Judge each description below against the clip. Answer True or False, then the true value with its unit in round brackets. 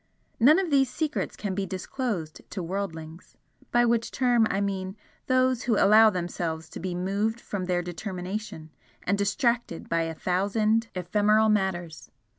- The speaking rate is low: False (150 wpm)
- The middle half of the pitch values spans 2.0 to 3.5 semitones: False (4.1 semitones)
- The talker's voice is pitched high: True (200 Hz)